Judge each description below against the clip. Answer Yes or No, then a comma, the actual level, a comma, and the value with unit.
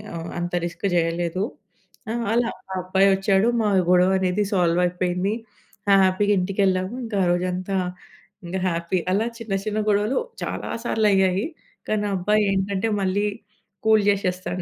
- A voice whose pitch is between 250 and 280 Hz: No, high, 190 Hz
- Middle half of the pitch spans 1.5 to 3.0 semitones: Yes, narrow, 2.4 semitones